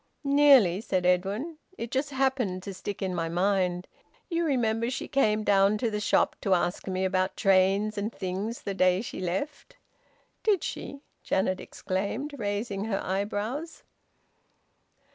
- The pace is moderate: Yes, average, 145 wpm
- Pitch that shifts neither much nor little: Yes, average, 4.7 semitones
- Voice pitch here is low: No, high, 205 Hz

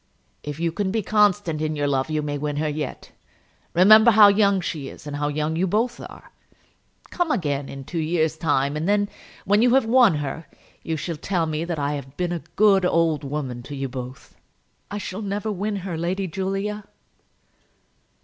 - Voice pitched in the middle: Yes, medium, 165 Hz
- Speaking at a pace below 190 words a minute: No, average, 195 wpm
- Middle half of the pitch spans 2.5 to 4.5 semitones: No, wide, 5.4 semitones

